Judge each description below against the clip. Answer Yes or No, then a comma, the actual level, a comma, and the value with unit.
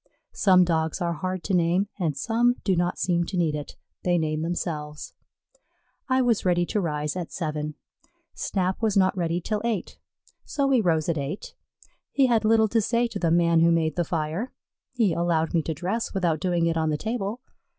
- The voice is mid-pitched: Yes, medium, 175 Hz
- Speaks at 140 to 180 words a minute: No, average, 195 wpm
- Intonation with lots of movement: No, average, 4.1 semitones